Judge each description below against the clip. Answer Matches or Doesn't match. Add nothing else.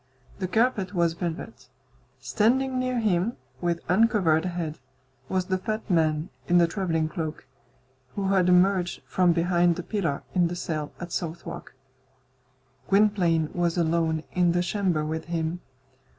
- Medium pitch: Matches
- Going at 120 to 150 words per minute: Matches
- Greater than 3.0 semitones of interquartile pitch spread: Doesn't match